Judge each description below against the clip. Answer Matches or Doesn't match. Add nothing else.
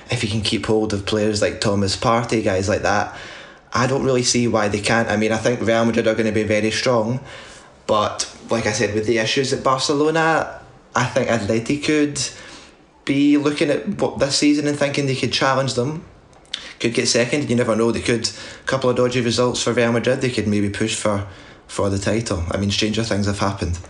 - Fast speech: Matches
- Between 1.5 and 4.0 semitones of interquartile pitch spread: Matches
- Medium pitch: Doesn't match